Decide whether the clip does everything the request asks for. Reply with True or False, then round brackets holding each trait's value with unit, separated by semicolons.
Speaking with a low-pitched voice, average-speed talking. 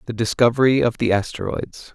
True (115 Hz; 155 wpm)